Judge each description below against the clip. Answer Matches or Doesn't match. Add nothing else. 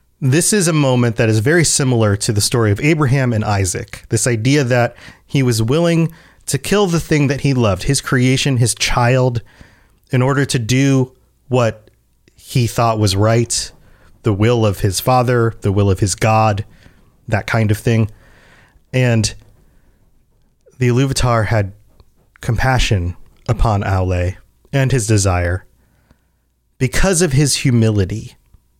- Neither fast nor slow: Matches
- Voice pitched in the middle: Doesn't match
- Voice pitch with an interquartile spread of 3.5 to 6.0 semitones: Matches